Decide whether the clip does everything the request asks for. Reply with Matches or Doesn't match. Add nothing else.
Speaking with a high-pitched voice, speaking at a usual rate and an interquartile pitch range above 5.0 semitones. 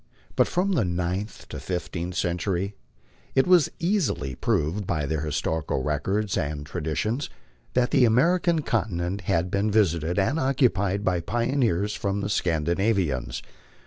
Doesn't match